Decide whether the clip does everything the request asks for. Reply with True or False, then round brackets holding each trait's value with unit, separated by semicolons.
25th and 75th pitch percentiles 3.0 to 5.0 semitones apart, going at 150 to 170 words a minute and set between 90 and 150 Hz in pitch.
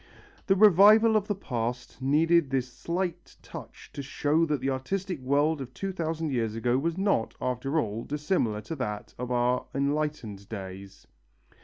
False (5.6 semitones; 160 wpm; 140 Hz)